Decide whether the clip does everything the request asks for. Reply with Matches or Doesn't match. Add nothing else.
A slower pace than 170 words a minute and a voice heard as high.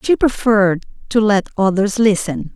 Matches